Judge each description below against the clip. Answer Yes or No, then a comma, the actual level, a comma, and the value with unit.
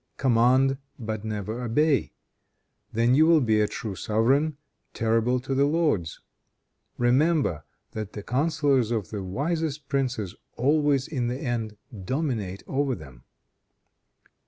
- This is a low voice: Yes, low, 125 Hz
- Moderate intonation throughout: Yes, average, 4.6 semitones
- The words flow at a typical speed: No, slow, 125 wpm